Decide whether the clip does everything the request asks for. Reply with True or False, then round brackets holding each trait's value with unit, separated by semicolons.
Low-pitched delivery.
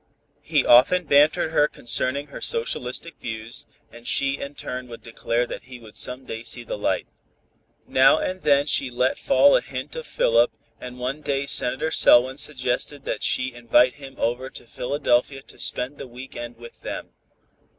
True (130 Hz)